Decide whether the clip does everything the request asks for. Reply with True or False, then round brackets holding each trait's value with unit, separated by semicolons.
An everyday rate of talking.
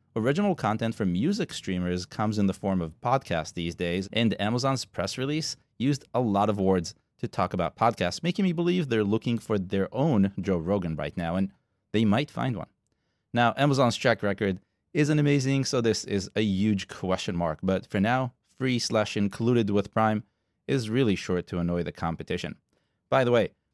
True (185 wpm)